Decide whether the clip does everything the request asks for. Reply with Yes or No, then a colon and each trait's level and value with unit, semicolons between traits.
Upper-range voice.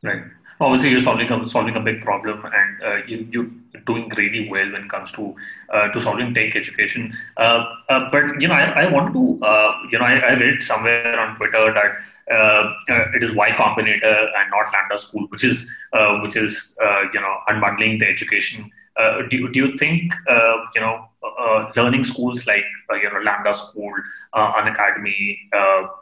No: low, 110 Hz